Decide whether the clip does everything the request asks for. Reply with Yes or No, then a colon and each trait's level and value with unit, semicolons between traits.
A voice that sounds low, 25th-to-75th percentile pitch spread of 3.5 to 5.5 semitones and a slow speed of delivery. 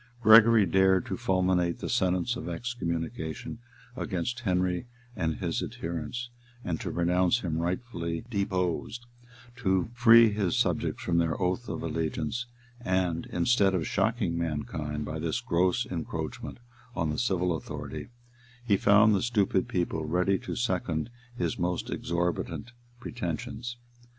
Yes: very low, 90 Hz; average, 5.0 semitones; slow, 130 wpm